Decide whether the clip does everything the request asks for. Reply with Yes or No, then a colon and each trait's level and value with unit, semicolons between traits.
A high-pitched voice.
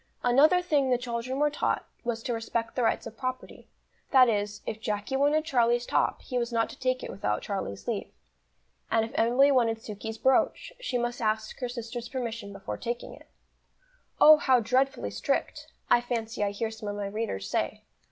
Yes: high, 235 Hz